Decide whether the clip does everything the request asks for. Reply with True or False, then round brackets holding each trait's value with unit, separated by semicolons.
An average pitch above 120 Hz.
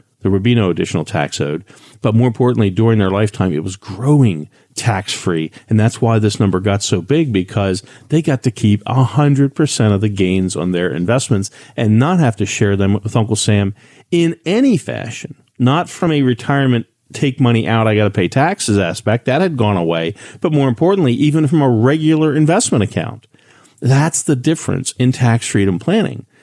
False (115 Hz)